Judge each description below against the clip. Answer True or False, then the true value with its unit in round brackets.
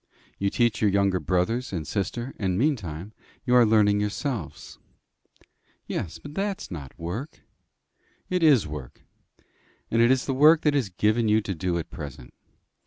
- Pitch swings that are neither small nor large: False (6.0 semitones)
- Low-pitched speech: True (105 Hz)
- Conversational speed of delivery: True (160 wpm)